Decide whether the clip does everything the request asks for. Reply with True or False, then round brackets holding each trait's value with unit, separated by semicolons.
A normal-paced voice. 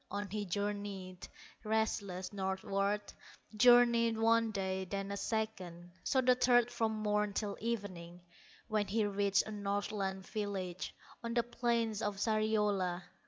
False (130 wpm)